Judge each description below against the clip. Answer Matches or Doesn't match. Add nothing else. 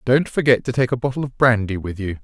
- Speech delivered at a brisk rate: Matches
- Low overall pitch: Matches